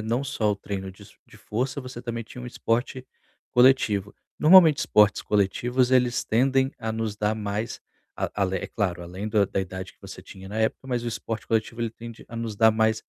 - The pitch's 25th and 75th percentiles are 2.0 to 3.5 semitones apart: Yes, average, 3.1 semitones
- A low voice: Yes, low, 110 Hz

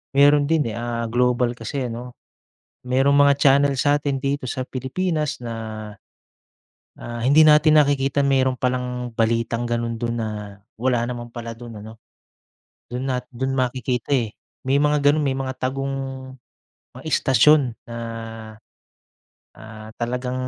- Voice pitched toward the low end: Yes, low, 130 Hz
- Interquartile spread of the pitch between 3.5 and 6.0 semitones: No, average, 2.9 semitones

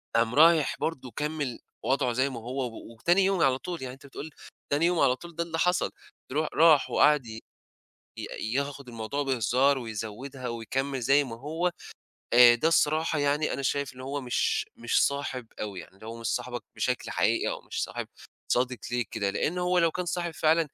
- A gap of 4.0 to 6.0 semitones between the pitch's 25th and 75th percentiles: Yes, average, 4.5 semitones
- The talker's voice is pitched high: No, low, 135 Hz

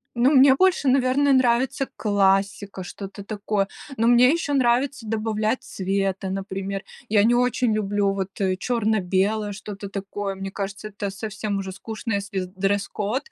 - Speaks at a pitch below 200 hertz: No, high, 205 Hz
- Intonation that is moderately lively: Yes, average, 3.4 semitones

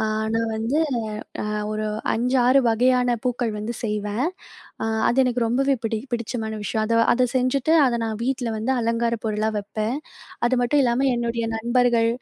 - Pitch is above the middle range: Yes, high, 235 Hz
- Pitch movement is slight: Yes, narrow, 2.1 semitones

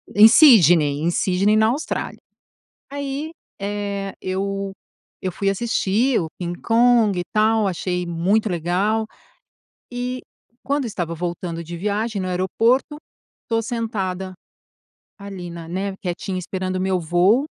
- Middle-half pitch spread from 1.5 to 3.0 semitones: No, average, 3.9 semitones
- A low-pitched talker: No, high, 195 Hz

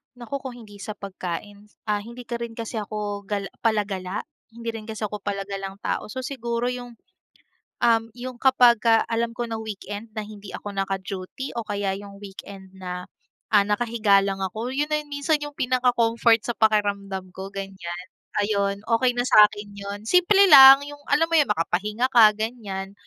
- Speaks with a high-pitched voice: Yes, high, 215 Hz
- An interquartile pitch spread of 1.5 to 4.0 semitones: Yes, average, 3.3 semitones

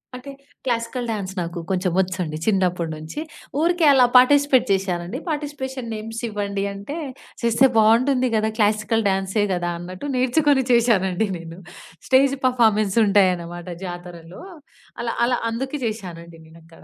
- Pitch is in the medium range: No, high, 215 Hz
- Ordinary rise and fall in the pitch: No, wide, 5.7 semitones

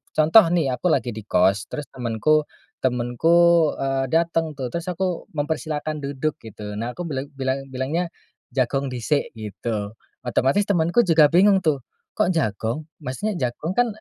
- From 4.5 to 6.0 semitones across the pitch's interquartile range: Yes, average, 5.0 semitones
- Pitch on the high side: No, medium, 140 Hz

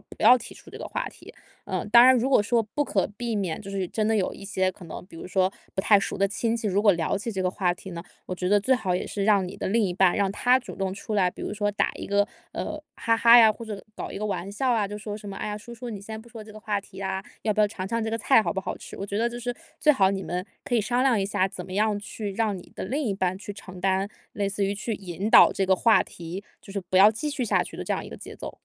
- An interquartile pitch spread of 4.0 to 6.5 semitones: No, average, 2.8 semitones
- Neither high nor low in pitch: No, high, 205 Hz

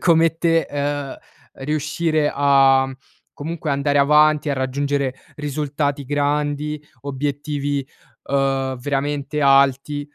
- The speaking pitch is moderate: Yes, medium, 145 Hz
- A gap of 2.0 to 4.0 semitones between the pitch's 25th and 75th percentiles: No, narrow, 1.4 semitones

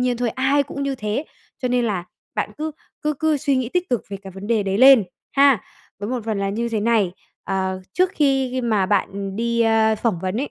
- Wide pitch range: No, average, 4.7 semitones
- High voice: Yes, high, 235 Hz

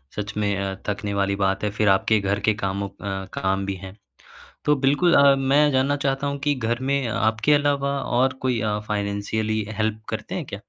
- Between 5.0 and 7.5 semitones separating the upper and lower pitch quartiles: Yes, average, 5.3 semitones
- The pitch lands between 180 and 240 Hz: No, low, 110 Hz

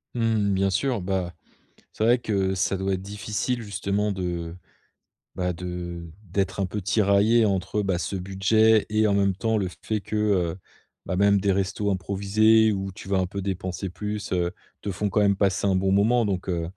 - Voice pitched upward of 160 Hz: No, low, 100 Hz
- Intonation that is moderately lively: No, narrow, 2.1 semitones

